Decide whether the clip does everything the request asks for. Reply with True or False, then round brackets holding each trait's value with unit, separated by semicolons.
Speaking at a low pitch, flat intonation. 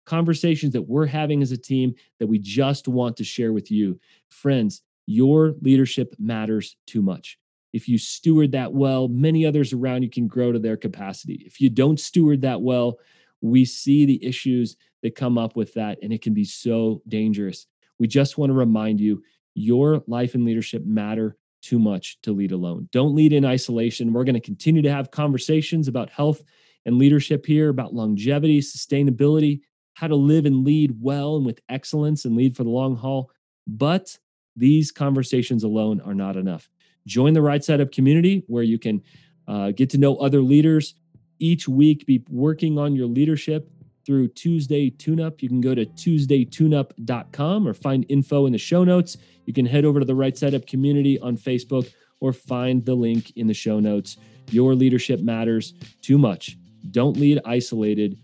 False (130 Hz; 4.0 semitones)